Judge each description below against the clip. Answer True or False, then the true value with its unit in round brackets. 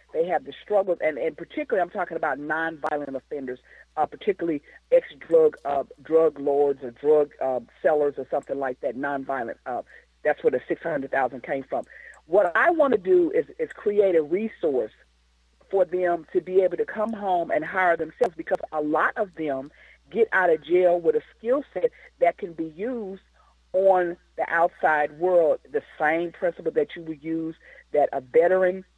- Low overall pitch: False (180 Hz)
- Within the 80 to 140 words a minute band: False (180 wpm)